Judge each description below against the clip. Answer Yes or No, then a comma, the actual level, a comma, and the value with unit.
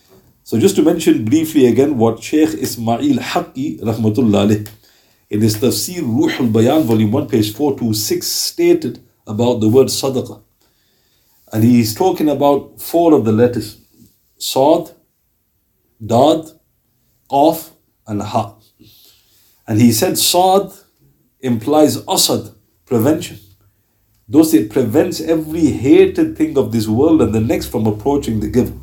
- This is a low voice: Yes, low, 120 Hz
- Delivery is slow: Yes, slow, 130 wpm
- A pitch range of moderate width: No, wide, 5.9 semitones